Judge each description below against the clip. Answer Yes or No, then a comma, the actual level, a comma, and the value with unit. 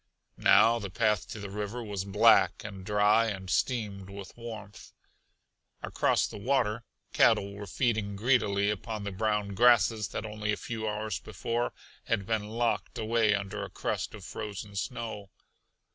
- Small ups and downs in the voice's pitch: Yes, narrow, 2.2 semitones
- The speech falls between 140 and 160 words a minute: Yes, average, 155 wpm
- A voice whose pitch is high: No, low, 105 Hz